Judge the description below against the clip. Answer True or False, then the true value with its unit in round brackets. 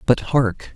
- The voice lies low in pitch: True (125 Hz)